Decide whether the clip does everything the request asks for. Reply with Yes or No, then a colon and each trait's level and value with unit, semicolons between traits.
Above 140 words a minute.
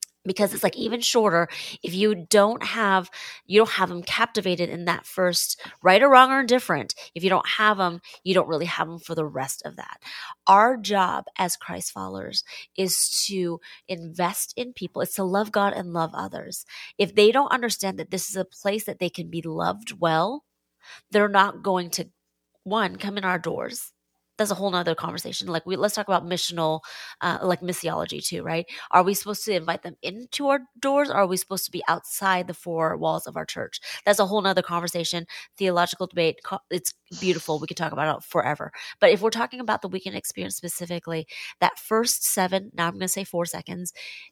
Yes: fast, 205 wpm